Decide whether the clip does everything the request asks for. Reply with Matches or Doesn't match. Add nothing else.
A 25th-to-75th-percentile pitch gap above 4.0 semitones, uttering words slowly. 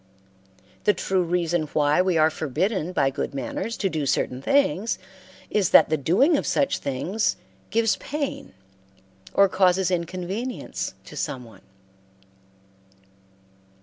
Matches